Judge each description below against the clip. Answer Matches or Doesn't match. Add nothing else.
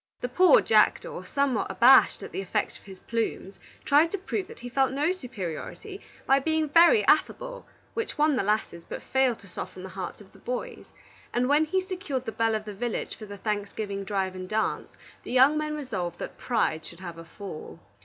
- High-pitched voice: Matches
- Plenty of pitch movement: Matches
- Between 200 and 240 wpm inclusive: Matches